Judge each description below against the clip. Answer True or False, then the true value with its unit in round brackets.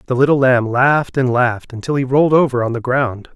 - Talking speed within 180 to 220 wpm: False (230 wpm)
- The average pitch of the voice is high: False (130 Hz)